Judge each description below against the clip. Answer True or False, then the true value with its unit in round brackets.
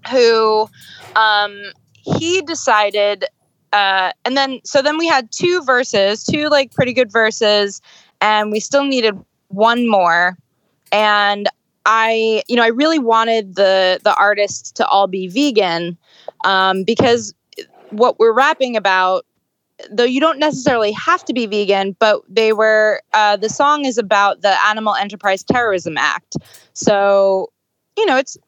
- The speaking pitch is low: False (215 Hz)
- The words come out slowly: False (145 wpm)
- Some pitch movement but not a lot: True (4.2 semitones)